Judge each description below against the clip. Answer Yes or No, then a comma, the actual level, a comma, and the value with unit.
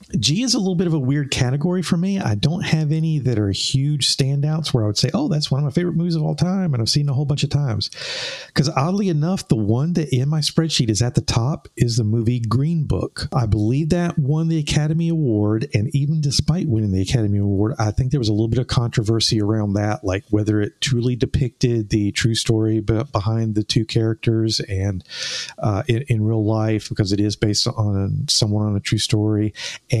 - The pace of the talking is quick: Yes, fast, 230 wpm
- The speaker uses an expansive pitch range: Yes, wide, 5.8 semitones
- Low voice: Yes, low, 125 Hz